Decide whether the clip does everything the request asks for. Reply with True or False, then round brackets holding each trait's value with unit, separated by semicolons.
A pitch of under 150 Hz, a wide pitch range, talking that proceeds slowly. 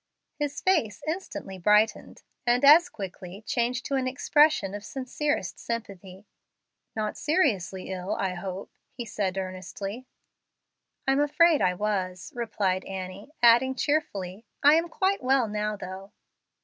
False (215 Hz; 6.3 semitones; 130 wpm)